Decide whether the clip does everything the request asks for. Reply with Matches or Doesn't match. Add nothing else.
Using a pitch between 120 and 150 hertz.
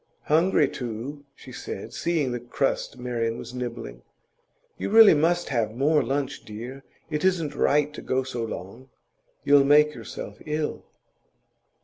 Matches